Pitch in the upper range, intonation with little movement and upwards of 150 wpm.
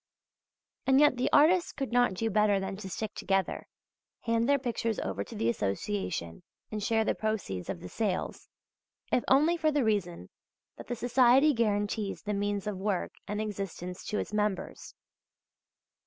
No: high, 210 Hz; average, 4.1 semitones; average, 165 wpm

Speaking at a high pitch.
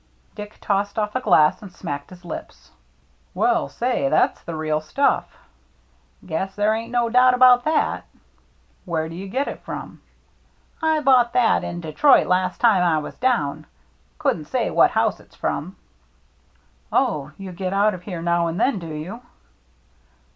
Yes: high, 195 Hz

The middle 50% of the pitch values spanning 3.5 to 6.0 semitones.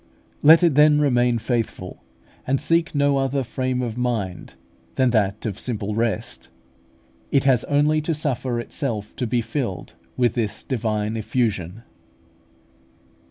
Yes: average, 4.2 semitones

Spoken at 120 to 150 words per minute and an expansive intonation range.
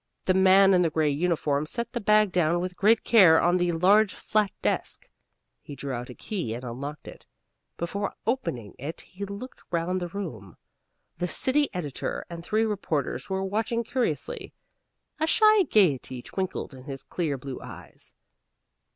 No: average, 165 wpm; wide, 6.0 semitones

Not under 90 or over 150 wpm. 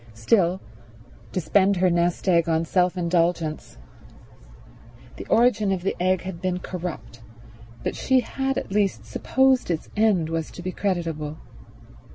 Yes: average, 145 wpm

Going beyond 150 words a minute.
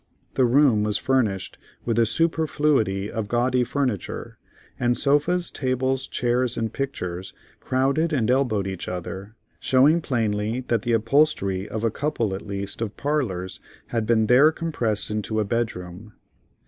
No: average, 145 wpm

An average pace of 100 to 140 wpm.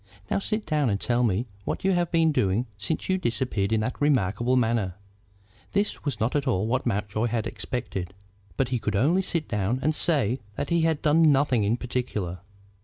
No: average, 195 wpm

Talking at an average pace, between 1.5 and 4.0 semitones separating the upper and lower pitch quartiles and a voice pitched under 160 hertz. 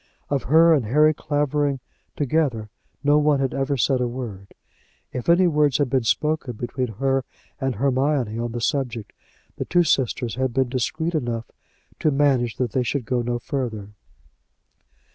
Yes: average, 160 wpm; average, 3.5 semitones; low, 135 Hz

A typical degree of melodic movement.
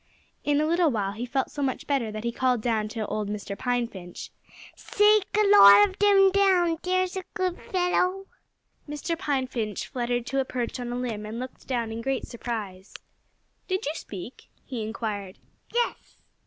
No: wide, 8.3 semitones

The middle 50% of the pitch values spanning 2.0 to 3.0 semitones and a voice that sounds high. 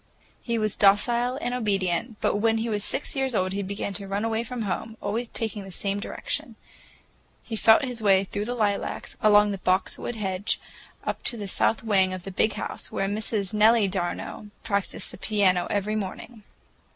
Yes: narrow, 2.4 semitones; high, 210 Hz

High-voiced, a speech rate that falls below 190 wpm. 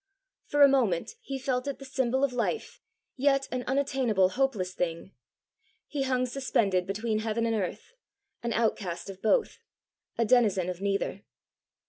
Yes: high, 235 Hz; average, 150 wpm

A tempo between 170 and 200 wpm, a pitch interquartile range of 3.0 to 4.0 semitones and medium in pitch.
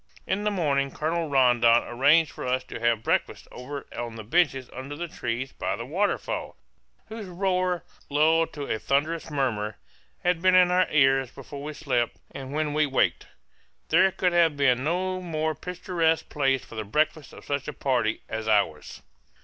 No: average, 175 wpm; average, 5.0 semitones; medium, 145 Hz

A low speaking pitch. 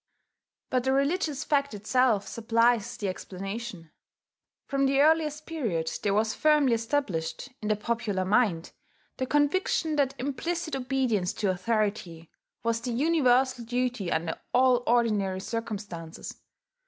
No: high, 235 Hz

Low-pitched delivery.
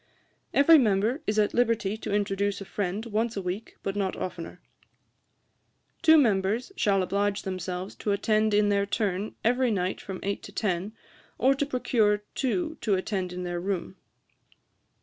No: high, 205 Hz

